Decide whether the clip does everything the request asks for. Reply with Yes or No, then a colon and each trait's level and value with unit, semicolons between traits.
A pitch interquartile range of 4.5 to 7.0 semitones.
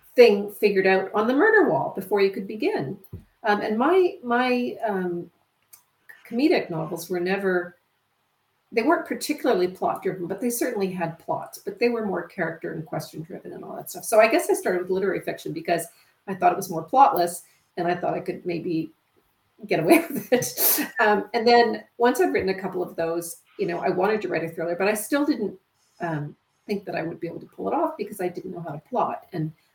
Yes: wide, 5.5 semitones